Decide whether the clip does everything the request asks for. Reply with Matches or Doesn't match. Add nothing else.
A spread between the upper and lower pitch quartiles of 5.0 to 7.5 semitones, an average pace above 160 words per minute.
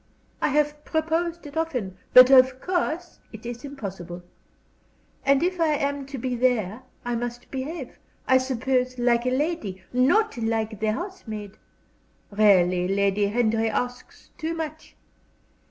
Doesn't match